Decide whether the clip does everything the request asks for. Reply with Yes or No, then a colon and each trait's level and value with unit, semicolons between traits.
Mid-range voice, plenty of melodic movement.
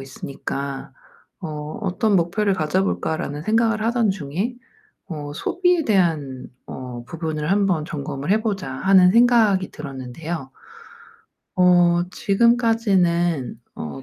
Yes: medium, 175 Hz; wide, 6.0 semitones